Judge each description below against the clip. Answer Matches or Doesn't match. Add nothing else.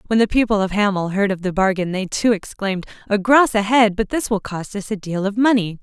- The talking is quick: Matches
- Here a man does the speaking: Doesn't match